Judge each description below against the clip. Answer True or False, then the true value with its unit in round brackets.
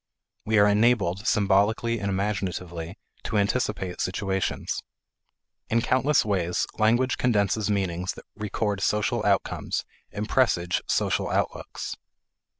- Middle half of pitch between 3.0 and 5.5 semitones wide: False (2.6 semitones)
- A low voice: True (105 Hz)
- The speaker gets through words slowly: True (110 wpm)